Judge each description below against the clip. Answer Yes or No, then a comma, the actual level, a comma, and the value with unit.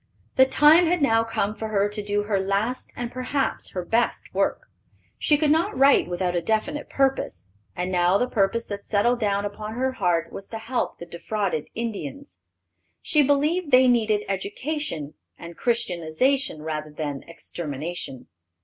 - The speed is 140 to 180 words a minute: Yes, average, 160 wpm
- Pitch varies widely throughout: Yes, wide, 6.5 semitones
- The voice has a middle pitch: No, high, 210 Hz